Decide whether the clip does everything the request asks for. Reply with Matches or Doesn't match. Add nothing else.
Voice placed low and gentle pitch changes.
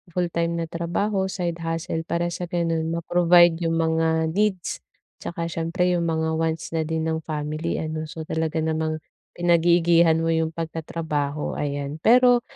Doesn't match